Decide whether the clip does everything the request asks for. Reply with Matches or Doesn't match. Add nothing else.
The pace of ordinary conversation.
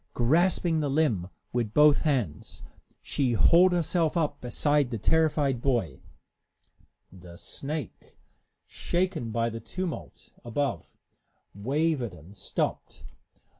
Doesn't match